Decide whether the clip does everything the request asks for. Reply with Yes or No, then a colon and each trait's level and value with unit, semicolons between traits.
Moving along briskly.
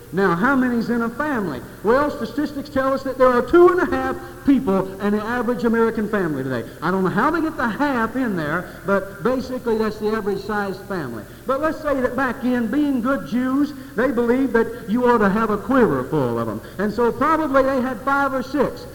Yes: fast, 220 wpm